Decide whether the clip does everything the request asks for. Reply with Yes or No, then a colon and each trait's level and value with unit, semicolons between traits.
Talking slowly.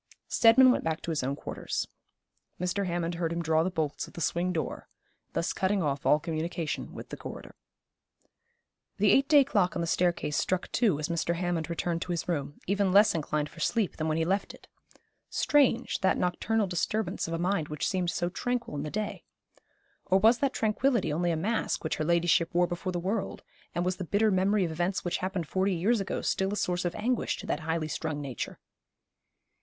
No: fast, 205 wpm